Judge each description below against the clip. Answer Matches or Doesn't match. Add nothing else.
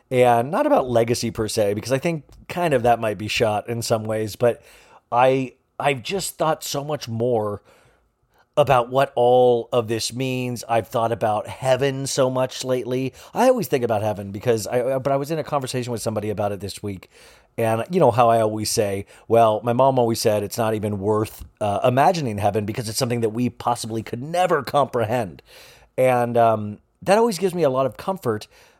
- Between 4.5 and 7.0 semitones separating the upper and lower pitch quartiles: Doesn't match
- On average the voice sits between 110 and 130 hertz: Matches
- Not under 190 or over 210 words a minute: Matches